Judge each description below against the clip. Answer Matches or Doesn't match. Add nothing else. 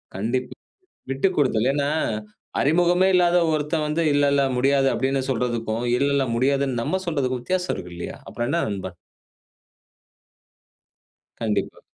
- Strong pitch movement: Doesn't match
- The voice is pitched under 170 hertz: Matches